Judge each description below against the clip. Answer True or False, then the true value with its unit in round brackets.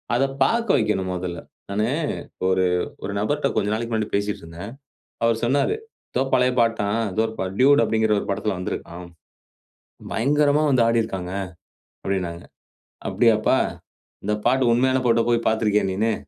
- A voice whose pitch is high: False (110 Hz)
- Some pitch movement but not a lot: True (3.5 semitones)